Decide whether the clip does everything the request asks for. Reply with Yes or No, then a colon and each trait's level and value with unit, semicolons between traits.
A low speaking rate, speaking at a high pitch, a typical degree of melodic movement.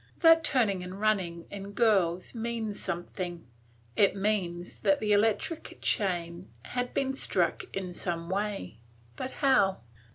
Yes: slow, 130 wpm; high, 200 Hz; average, 3.8 semitones